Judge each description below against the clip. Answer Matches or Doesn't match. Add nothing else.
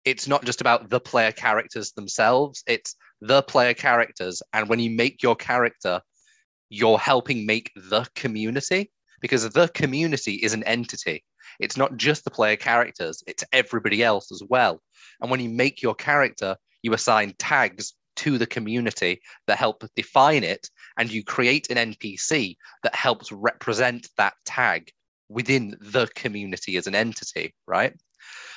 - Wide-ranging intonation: Doesn't match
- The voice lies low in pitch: Matches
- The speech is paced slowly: Doesn't match